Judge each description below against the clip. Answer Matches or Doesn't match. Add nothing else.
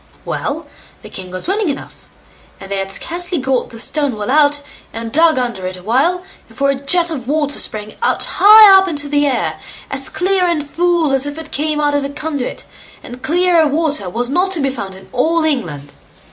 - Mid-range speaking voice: Doesn't match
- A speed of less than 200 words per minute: Doesn't match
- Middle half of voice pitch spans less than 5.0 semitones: Doesn't match